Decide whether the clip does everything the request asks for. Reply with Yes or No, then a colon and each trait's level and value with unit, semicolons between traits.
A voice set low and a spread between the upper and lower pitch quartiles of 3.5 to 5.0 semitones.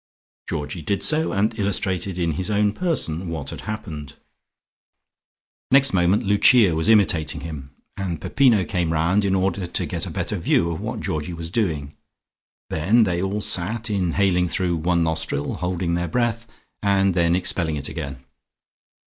Yes: very low, 90 Hz; average, 3.8 semitones